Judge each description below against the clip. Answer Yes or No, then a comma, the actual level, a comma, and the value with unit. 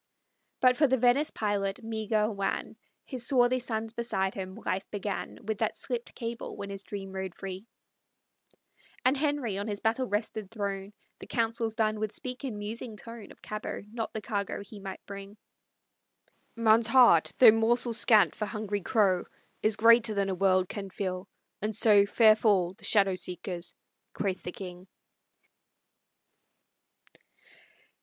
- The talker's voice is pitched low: No, high, 215 Hz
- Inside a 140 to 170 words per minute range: Yes, average, 150 wpm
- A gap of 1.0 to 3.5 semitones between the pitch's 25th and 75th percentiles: Yes, average, 2.8 semitones